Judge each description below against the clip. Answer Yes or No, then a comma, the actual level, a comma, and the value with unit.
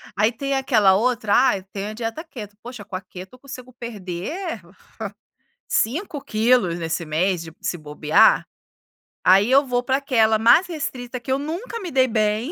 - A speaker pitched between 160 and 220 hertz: No, high, 230 Hz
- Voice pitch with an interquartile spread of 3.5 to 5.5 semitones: Yes, average, 5.1 semitones